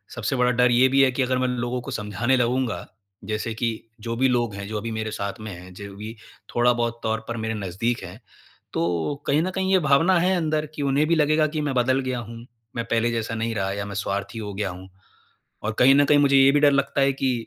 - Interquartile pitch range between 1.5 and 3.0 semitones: No, average, 4.3 semitones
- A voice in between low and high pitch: No, low, 120 Hz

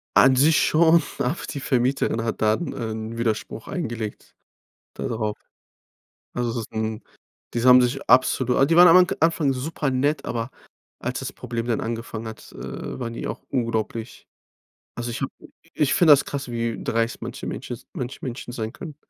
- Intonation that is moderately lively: Yes, average, 3.2 semitones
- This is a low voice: Yes, low, 125 Hz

